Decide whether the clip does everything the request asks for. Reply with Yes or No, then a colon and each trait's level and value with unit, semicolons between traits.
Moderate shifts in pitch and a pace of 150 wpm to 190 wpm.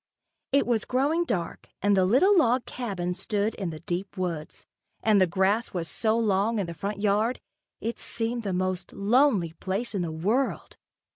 Yes: average, 4.1 semitones; average, 175 wpm